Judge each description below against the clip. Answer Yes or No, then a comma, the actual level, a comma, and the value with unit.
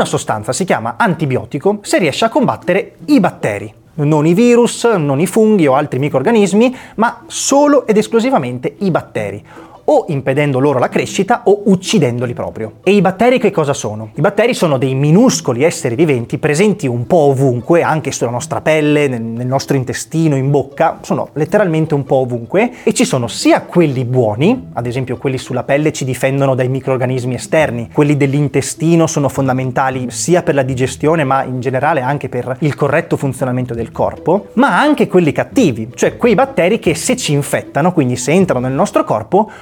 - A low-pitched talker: No, medium, 145 Hz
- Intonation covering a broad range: Yes, wide, 6.5 semitones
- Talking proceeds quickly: Yes, fast, 175 wpm